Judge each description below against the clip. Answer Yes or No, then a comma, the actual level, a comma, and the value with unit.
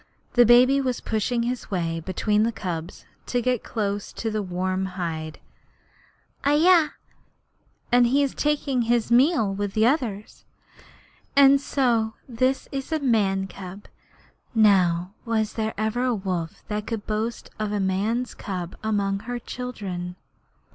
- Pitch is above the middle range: Yes, high, 220 Hz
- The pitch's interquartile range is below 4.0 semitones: No, average, 4.3 semitones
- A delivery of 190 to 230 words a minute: No, average, 140 wpm